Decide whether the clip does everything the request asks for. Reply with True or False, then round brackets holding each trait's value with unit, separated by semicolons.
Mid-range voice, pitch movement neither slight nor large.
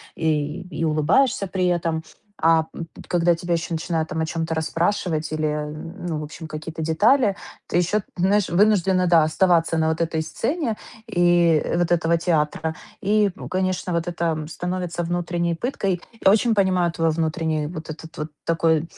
False (170 Hz; 2.3 semitones)